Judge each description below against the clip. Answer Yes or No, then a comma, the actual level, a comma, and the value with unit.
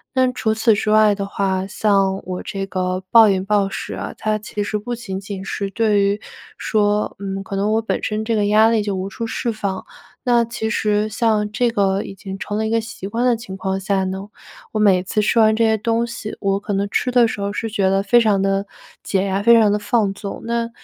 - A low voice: No, high, 210 Hz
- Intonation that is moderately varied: No, narrow, 2.3 semitones